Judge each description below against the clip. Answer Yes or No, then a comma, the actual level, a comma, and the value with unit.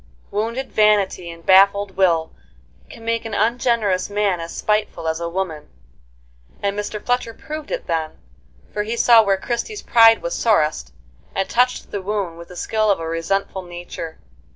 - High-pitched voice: Yes, high, 200 Hz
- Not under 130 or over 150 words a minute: No, average, 165 wpm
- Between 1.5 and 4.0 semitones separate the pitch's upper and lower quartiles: No, average, 4.4 semitones